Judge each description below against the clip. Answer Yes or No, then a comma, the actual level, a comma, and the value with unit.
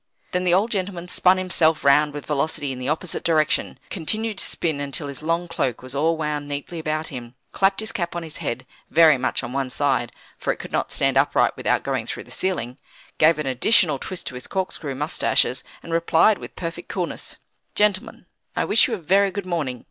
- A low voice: No, medium, 160 Hz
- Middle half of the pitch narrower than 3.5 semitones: No, average, 4.5 semitones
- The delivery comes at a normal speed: No, fast, 210 wpm